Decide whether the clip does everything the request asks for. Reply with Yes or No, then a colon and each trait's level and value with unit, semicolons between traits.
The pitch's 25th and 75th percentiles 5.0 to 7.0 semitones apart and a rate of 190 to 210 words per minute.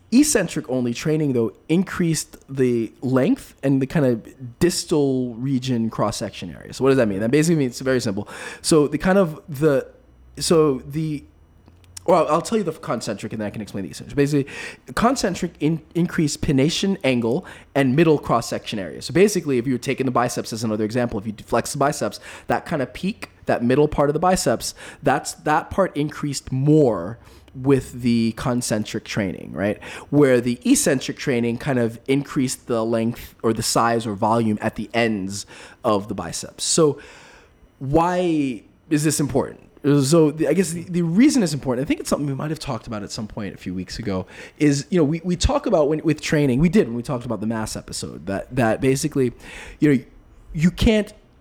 Yes: wide, 5.4 semitones; average, 200 wpm